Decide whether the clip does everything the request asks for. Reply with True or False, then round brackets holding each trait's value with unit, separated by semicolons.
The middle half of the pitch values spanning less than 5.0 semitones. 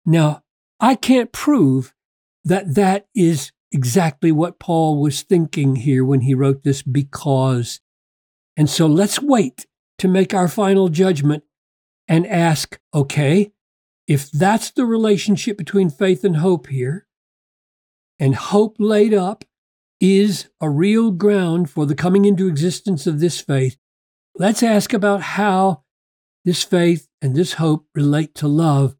False (5.5 semitones)